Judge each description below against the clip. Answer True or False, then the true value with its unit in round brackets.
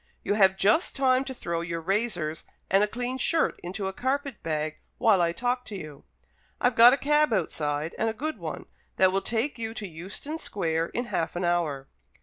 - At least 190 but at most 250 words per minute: True (200 wpm)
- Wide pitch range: True (6.5 semitones)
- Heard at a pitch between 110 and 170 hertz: False (200 Hz)